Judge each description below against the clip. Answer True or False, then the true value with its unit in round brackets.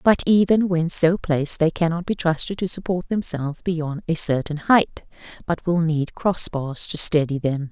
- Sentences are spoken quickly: False (185 wpm)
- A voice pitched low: False (165 Hz)